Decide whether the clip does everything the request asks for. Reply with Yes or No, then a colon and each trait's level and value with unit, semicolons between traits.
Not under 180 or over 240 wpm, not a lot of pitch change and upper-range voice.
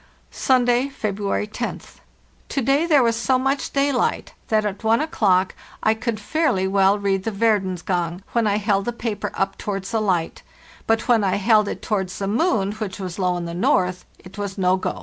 No: average, 195 wpm; average, 3.6 semitones; high, 205 Hz